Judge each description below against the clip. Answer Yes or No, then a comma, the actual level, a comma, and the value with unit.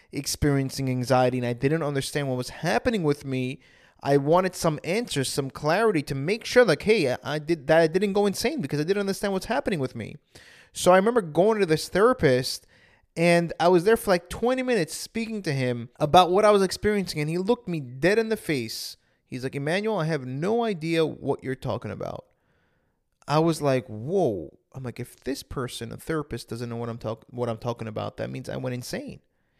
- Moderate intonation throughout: No, wide, 7.0 semitones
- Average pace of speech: No, fast, 215 wpm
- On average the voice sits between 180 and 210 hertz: No, medium, 155 Hz